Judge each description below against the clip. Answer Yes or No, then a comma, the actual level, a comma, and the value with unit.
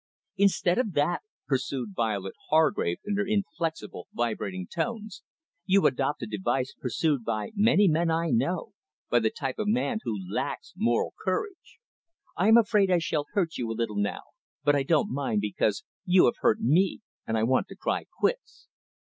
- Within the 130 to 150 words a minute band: No, average, 170 wpm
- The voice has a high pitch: No, medium, 155 Hz